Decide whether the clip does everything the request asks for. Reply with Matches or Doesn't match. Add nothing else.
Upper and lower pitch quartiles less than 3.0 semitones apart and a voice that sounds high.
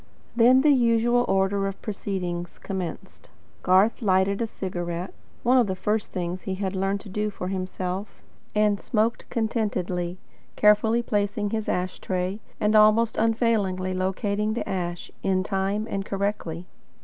Matches